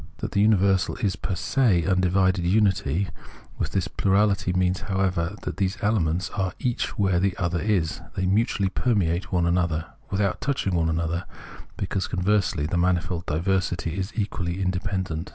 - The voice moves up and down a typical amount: No, narrow, 2.3 semitones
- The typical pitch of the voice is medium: No, very low, 95 Hz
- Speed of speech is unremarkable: Yes, average, 160 wpm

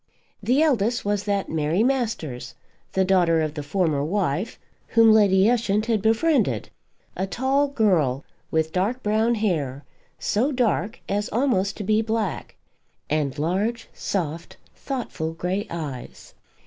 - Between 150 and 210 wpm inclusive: No, slow, 135 wpm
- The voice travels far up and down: Yes, wide, 5.7 semitones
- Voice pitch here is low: No, high, 200 Hz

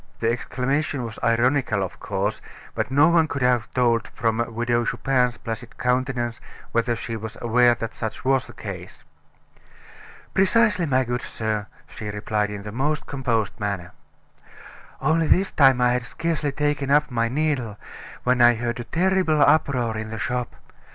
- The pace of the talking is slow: No, average, 165 wpm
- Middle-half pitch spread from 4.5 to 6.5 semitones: No, average, 3.8 semitones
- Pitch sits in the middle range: No, low, 125 Hz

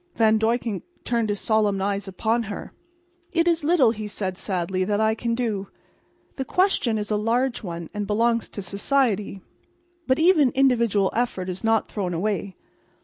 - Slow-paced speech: No, average, 165 wpm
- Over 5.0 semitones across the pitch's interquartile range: No, average, 3.3 semitones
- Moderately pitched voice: No, high, 220 Hz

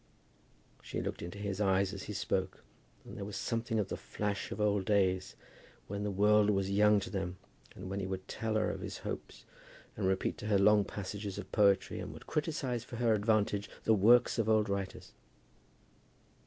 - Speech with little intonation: Yes, narrow, 1.7 semitones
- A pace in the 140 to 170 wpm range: No, average, 195 wpm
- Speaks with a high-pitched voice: No, low, 100 Hz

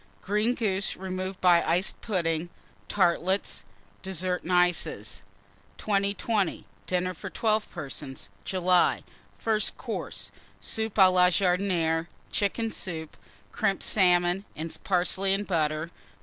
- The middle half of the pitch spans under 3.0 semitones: Yes, narrow, 2.4 semitones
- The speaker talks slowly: Yes, slow, 115 wpm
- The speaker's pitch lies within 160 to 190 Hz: Yes, medium, 185 Hz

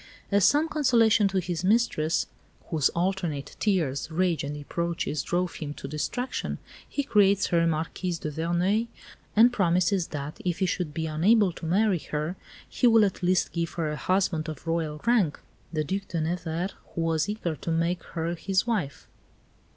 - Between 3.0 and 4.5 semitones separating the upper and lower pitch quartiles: Yes, average, 3.7 semitones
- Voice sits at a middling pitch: Yes, medium, 175 Hz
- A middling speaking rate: Yes, average, 170 wpm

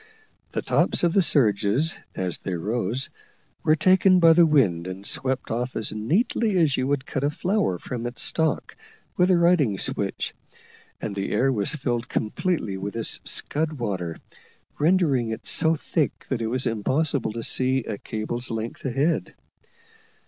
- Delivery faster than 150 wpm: Yes, average, 165 wpm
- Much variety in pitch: Yes, wide, 6.5 semitones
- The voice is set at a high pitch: No, low, 130 Hz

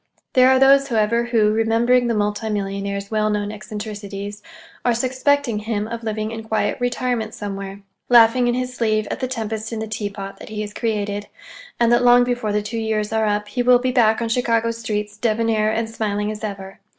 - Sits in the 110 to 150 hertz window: No, high, 220 Hz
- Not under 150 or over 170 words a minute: No, average, 200 wpm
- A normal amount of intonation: No, narrow, 2.2 semitones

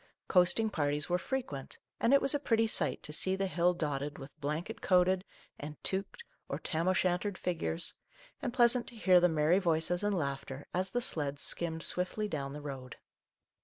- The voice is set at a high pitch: No, medium, 175 Hz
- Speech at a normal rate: Yes, average, 185 wpm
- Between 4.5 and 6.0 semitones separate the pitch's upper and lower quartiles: Yes, average, 4.8 semitones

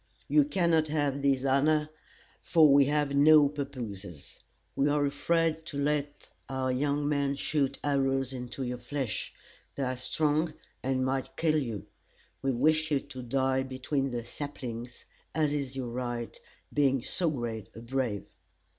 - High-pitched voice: No, medium, 140 Hz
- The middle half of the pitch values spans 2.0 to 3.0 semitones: Yes, narrow, 2.4 semitones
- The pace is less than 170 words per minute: Yes, average, 150 wpm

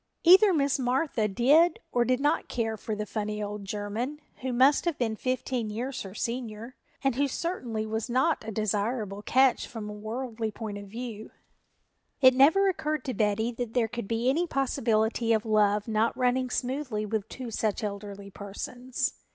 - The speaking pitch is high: Yes, high, 235 Hz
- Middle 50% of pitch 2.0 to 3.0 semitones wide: No, average, 3.5 semitones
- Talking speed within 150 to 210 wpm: Yes, average, 175 wpm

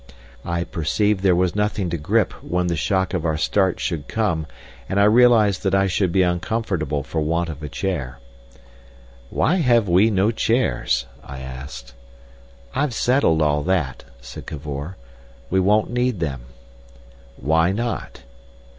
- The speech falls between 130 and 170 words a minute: Yes, average, 150 wpm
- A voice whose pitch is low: Yes, very low, 90 Hz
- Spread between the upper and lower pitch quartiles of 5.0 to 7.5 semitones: Yes, average, 5.3 semitones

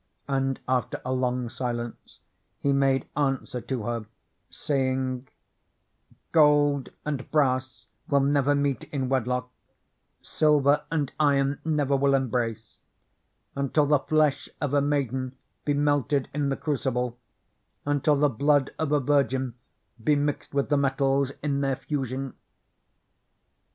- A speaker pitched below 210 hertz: Yes, low, 135 Hz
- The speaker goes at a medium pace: No, slow, 125 wpm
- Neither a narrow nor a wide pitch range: No, narrow, 1.9 semitones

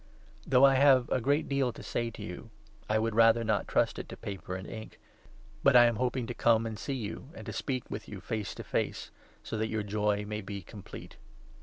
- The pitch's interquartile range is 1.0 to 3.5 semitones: Yes, average, 3.1 semitones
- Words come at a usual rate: No, fast, 230 wpm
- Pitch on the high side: No, low, 115 Hz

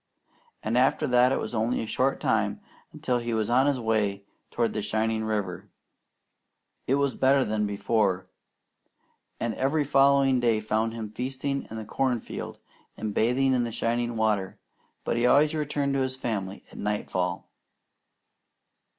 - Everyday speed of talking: Yes, average, 160 wpm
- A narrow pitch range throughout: No, average, 3.5 semitones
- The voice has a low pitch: Yes, low, 115 Hz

